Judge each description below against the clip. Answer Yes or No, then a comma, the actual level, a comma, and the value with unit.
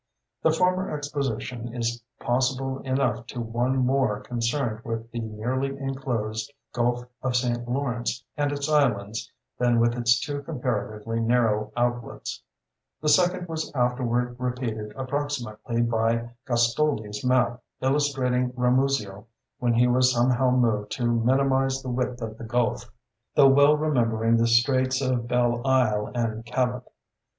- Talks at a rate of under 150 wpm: Yes, slow, 135 wpm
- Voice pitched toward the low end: Yes, low, 125 Hz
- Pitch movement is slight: Yes, narrow, 2.3 semitones